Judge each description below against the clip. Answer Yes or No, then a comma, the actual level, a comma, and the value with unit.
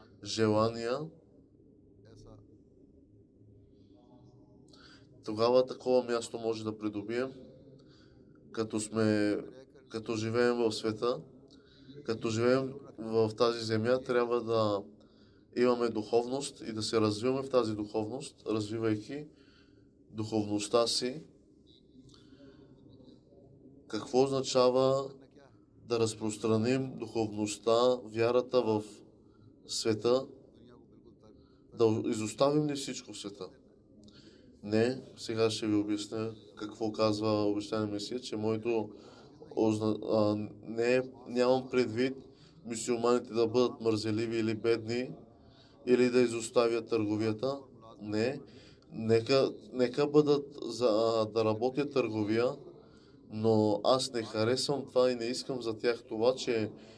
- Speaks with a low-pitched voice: Yes, low, 115 Hz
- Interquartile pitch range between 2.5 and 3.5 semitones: Yes, average, 3.0 semitones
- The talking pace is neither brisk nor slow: No, slow, 95 wpm